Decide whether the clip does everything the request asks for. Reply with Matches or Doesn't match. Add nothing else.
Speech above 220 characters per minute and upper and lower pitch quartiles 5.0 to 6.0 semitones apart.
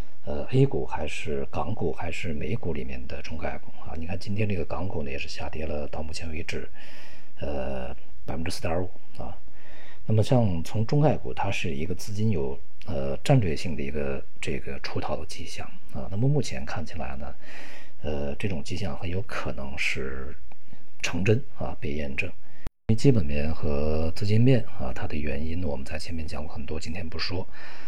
Matches